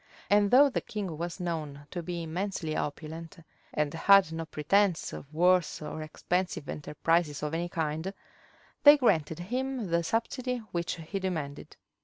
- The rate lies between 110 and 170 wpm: Yes, average, 150 wpm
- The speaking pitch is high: No, medium, 170 Hz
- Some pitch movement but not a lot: Yes, average, 4.0 semitones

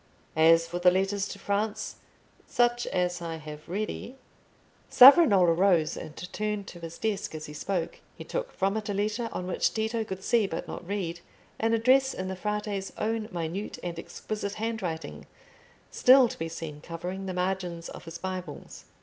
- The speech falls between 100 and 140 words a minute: No, average, 175 wpm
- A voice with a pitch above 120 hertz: Yes, high, 190 Hz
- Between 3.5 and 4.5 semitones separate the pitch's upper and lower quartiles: Yes, average, 4.1 semitones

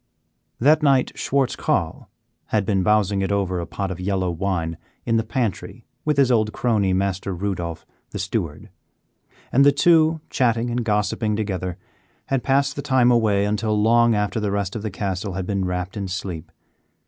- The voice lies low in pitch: Yes, low, 105 Hz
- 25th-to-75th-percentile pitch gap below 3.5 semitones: No, average, 3.9 semitones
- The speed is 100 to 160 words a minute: No, average, 175 wpm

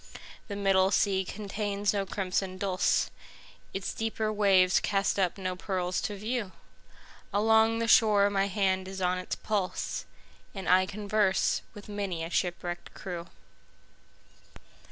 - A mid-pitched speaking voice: No, high, 195 Hz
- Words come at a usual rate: No, slow, 120 wpm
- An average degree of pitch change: No, narrow, 1.8 semitones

